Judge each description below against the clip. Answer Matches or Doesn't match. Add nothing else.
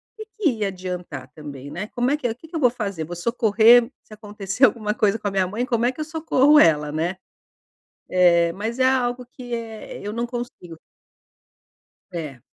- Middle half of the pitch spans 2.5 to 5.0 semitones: Doesn't match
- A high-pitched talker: Matches